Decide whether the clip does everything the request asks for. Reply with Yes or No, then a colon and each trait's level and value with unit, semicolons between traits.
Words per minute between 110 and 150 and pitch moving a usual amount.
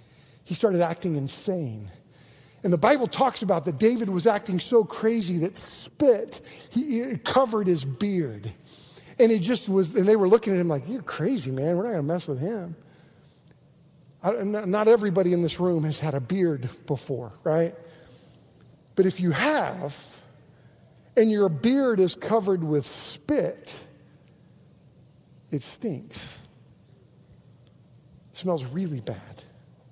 No: average, 140 wpm; wide, 5.7 semitones